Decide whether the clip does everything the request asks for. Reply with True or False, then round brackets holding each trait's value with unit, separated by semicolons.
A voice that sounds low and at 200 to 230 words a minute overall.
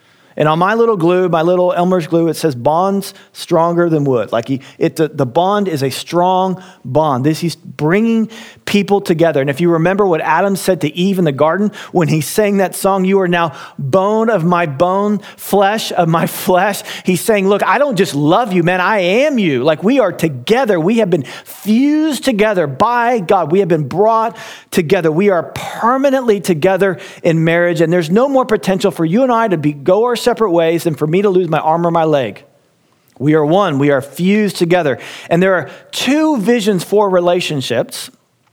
False (185 Hz; 205 wpm)